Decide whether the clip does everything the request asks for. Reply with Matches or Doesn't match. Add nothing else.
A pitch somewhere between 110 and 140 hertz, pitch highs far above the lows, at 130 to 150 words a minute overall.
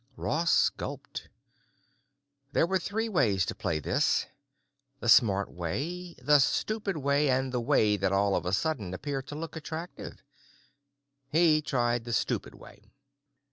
Matches